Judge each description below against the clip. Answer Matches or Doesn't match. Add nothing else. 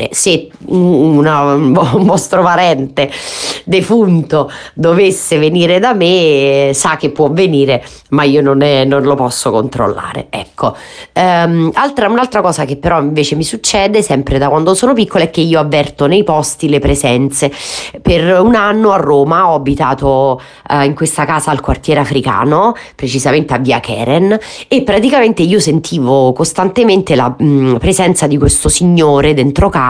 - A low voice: Doesn't match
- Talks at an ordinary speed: Matches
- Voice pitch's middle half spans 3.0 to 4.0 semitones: Doesn't match